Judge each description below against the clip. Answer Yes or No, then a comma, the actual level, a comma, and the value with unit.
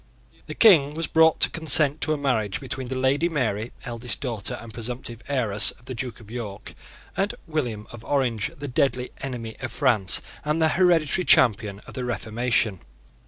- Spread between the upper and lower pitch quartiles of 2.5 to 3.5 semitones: No, average, 4.3 semitones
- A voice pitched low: Yes, low, 125 Hz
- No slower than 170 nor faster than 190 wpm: Yes, average, 175 wpm